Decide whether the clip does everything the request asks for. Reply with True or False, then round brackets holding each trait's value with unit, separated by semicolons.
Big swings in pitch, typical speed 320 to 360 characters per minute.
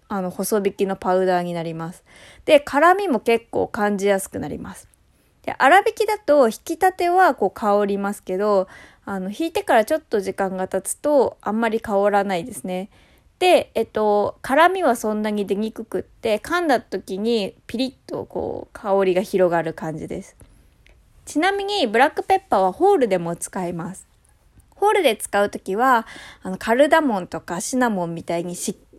True (7.5 semitones; 335 characters per minute)